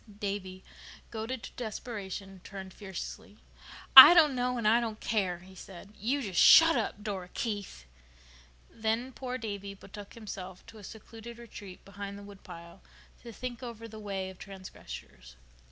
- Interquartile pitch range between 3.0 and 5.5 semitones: Yes, average, 3.4 semitones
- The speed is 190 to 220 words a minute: No, average, 155 wpm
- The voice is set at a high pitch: Yes, high, 205 Hz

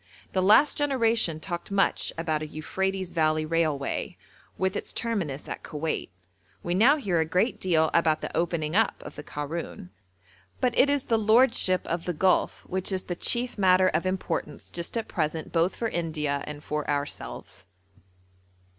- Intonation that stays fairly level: No, average, 4.4 semitones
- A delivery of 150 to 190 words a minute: Yes, average, 165 wpm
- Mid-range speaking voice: Yes, medium, 175 Hz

